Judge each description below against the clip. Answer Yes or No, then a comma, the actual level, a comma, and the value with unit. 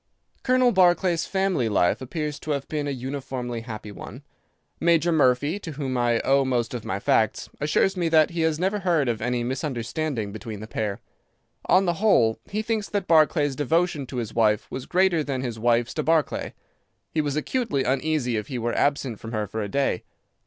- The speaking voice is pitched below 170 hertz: Yes, medium, 140 Hz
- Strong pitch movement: Yes, wide, 5.7 semitones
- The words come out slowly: No, average, 195 wpm